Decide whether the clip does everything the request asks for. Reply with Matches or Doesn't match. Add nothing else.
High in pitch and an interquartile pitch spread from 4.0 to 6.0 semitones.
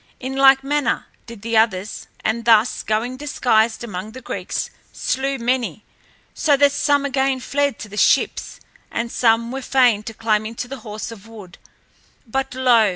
Doesn't match